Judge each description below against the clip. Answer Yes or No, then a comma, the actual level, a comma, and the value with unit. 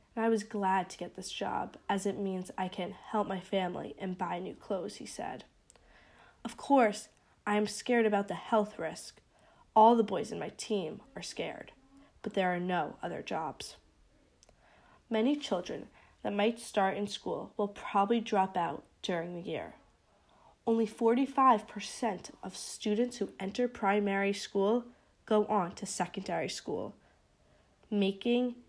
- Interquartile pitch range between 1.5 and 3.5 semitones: Yes, average, 3.0 semitones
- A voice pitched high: Yes, high, 205 Hz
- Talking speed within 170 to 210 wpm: No, average, 155 wpm